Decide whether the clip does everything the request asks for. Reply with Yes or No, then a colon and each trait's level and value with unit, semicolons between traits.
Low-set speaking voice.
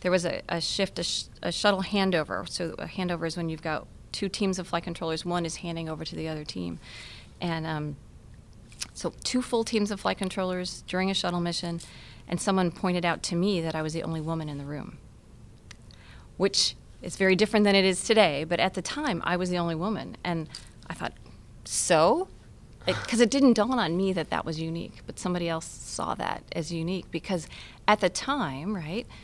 No: medium, 175 Hz